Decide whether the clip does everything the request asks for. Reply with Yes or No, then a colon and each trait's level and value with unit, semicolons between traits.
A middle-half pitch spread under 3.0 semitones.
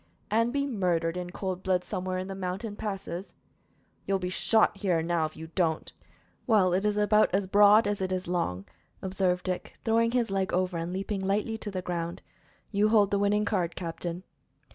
Yes: narrow, 2.5 semitones